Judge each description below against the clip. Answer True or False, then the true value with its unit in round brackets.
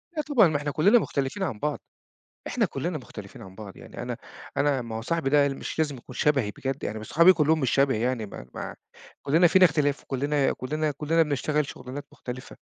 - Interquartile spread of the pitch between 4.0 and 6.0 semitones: False (3.5 semitones)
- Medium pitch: True (145 Hz)